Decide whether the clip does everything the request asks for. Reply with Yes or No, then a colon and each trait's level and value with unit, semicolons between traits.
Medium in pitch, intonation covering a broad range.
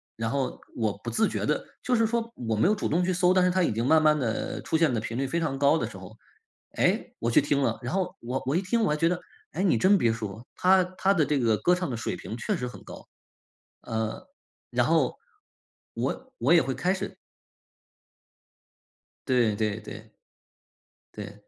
Yes: medium, 145 Hz; wide, 7.8 semitones